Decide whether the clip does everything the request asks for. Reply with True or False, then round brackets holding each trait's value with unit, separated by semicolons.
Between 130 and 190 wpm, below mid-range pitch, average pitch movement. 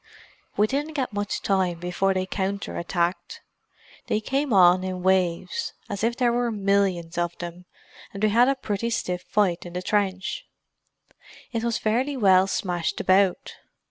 False (155 wpm; 195 Hz; 3.6 semitones)